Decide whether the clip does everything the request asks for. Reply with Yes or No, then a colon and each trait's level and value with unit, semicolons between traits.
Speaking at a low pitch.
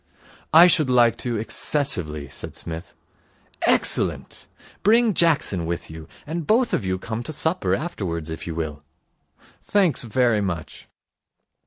Yes: low, 115 Hz